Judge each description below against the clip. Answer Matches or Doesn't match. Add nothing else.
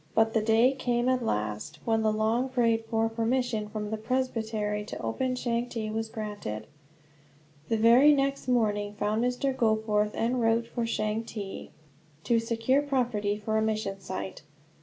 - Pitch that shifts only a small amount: Matches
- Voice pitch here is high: Matches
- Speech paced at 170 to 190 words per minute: Doesn't match